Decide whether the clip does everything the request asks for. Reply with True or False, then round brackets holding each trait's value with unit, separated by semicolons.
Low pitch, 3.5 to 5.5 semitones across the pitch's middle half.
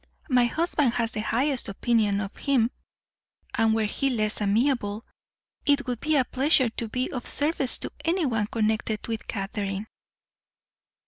False (235 Hz; 4.0 semitones)